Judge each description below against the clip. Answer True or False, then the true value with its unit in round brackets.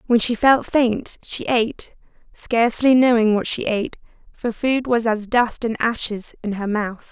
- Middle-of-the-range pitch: False (230 Hz)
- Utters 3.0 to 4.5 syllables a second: True (4.4 syllables/s)